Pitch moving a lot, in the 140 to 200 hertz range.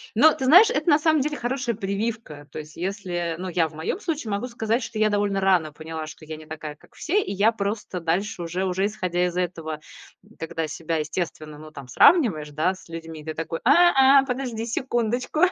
Yes: wide, 6.8 semitones; high, 190 Hz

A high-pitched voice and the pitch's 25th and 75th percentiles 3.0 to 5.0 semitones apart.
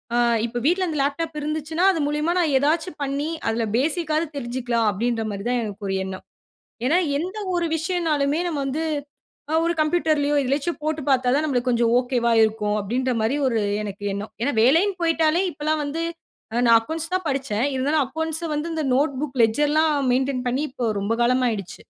Yes: very high, 280 Hz; average, 4.6 semitones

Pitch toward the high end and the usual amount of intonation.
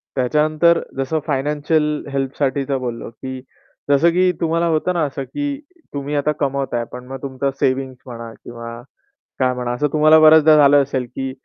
No: medium, 140 Hz; average, 3.0 semitones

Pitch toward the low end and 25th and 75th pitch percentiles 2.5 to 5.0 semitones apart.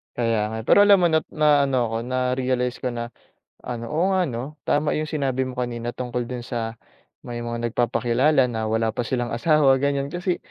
Yes: low, 125 Hz; average, 3.3 semitones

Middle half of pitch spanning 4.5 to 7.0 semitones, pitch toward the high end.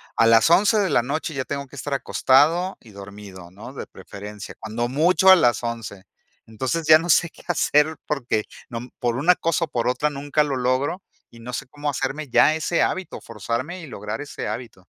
No: average, 5.1 semitones; low, 135 Hz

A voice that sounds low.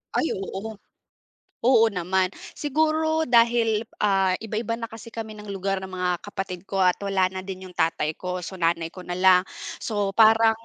No: high, 195 Hz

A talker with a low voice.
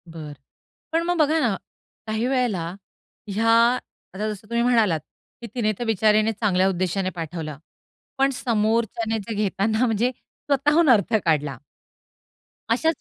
No: high, 220 Hz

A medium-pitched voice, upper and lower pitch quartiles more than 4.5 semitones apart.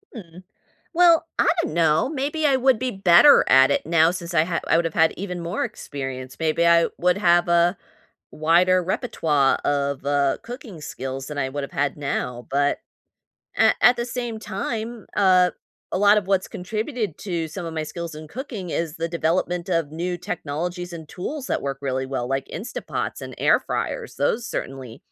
Yes: medium, 170 Hz; average, 5.2 semitones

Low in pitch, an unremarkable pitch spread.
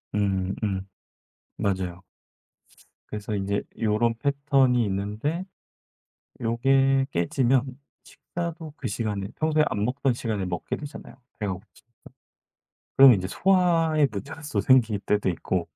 No: low, 115 Hz; wide, 5.7 semitones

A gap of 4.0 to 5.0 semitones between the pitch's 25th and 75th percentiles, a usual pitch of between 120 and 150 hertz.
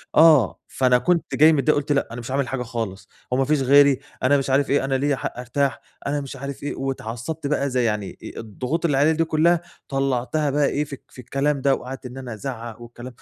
No: narrow, 2.5 semitones; low, 135 Hz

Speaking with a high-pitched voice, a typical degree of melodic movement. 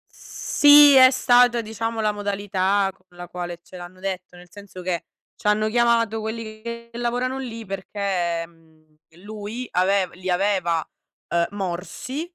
Yes: high, 205 Hz; average, 4.2 semitones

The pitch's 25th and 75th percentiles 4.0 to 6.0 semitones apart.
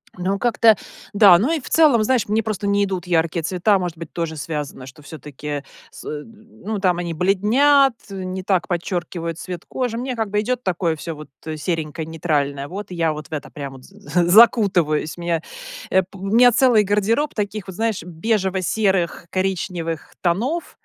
Yes: average, 4.6 semitones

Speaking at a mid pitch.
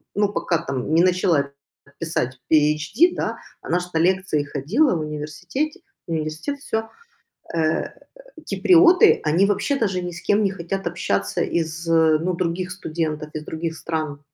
Yes: medium, 165 Hz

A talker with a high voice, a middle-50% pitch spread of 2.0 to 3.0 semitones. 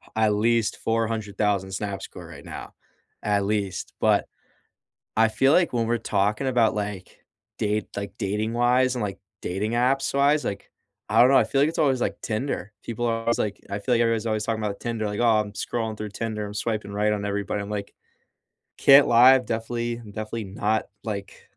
No: low, 110 Hz; narrow, 2.5 semitones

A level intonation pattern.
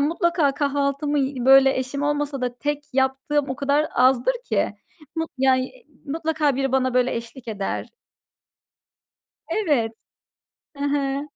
Yes: narrow, 2.1 semitones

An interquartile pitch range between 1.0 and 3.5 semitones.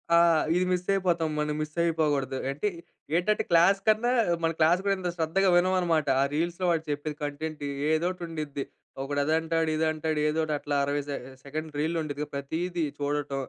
Yes: average, 2.8 semitones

